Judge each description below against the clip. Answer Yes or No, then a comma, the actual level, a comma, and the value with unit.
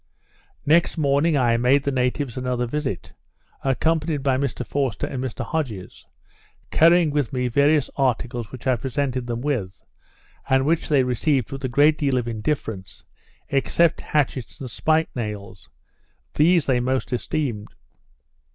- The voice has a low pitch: Yes, low, 130 Hz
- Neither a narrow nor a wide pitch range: Yes, average, 3.3 semitones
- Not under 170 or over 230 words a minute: No, average, 140 wpm